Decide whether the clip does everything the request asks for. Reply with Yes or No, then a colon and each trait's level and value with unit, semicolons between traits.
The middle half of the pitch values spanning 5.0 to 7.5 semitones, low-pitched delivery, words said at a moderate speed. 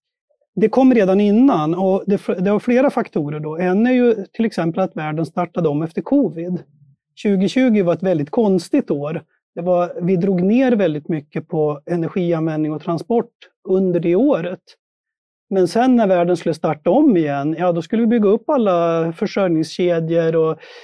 No: wide, 5.4 semitones; medium, 180 Hz; average, 165 wpm